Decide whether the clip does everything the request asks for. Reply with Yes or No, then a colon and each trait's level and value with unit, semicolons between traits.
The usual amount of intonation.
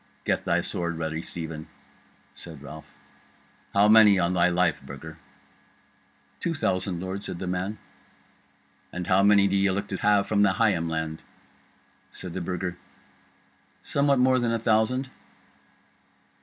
Yes: average, 3.4 semitones